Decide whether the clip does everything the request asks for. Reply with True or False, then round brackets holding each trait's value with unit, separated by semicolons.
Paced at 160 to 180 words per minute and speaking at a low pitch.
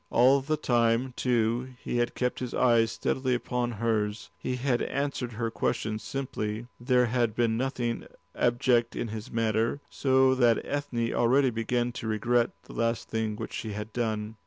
True (165 wpm; 120 Hz)